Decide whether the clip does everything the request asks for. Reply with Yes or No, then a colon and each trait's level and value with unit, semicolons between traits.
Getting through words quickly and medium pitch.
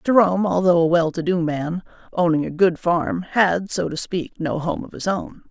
Yes: fast, 220 wpm; medium, 175 Hz